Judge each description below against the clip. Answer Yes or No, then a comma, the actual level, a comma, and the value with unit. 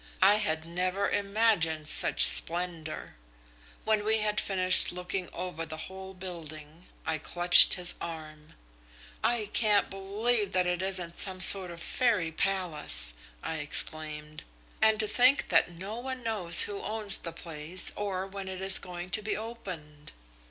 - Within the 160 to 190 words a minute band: No, average, 150 wpm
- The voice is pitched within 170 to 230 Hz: Yes, medium, 185 Hz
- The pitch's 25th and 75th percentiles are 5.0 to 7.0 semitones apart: No, average, 3.9 semitones